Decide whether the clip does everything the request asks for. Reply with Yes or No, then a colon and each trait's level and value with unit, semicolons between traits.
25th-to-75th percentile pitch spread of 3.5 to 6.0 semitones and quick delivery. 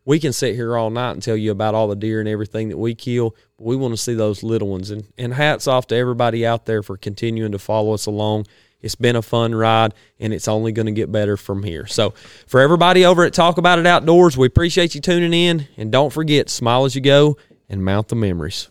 Yes: average, 4.1 semitones; fast, 255 wpm